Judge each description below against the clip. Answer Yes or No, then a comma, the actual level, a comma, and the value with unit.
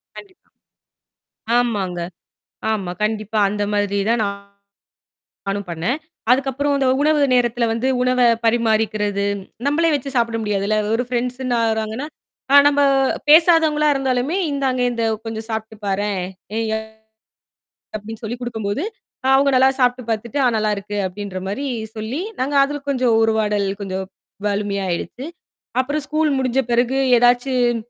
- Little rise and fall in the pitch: No, average, 4.1 semitones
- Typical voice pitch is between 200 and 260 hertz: Yes, high, 235 Hz